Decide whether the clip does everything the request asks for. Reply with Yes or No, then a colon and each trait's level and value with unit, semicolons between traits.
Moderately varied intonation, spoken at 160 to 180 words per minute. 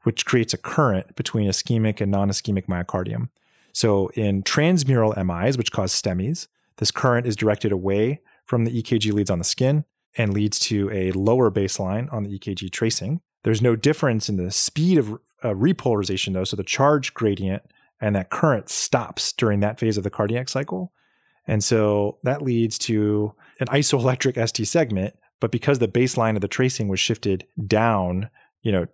Yes: average, 3.8 semitones; average, 175 wpm